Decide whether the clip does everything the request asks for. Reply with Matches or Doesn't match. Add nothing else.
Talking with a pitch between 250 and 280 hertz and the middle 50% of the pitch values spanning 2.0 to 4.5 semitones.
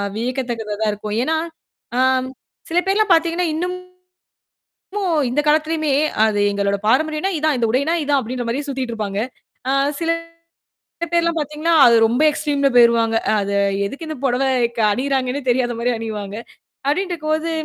Doesn't match